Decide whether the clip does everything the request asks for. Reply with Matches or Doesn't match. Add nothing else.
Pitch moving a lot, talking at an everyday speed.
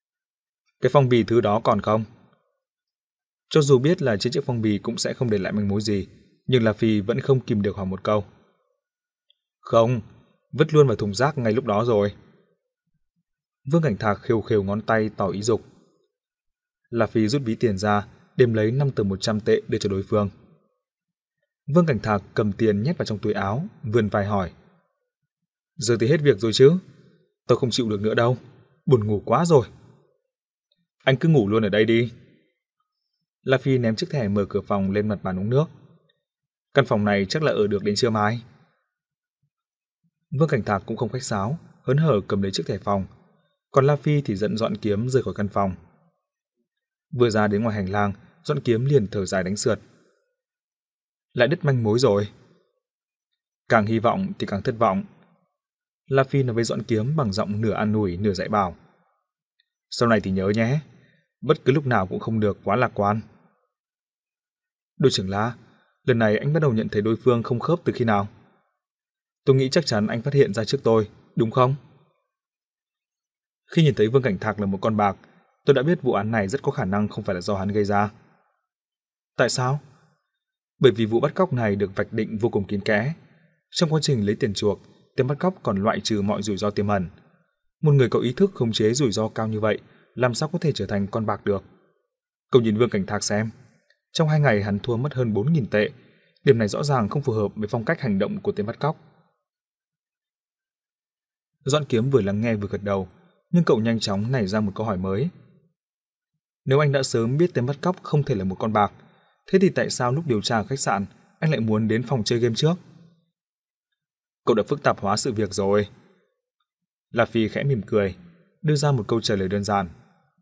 Matches